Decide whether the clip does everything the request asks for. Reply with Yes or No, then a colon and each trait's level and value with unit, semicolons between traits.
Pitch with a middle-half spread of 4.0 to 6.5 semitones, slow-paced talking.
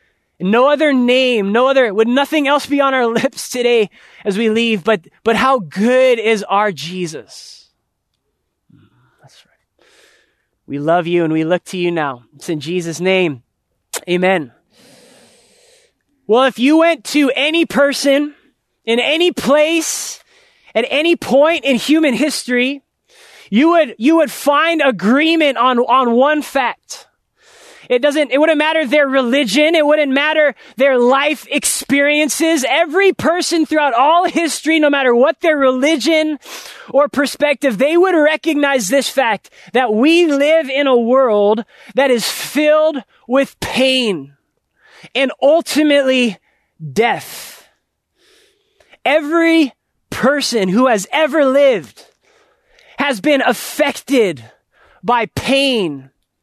Yes: average, 4.6 semitones; slow, 130 wpm